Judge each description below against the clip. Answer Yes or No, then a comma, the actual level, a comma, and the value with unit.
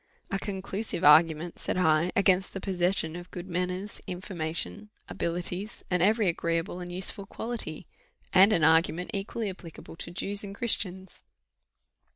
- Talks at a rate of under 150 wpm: Yes, average, 140 wpm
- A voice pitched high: No, medium, 180 Hz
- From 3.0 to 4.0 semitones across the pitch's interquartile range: No, narrow, 2.6 semitones